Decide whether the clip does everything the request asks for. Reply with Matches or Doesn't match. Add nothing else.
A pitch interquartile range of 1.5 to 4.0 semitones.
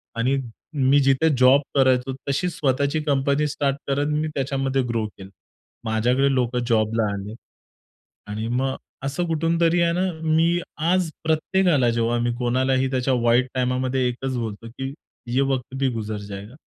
Matches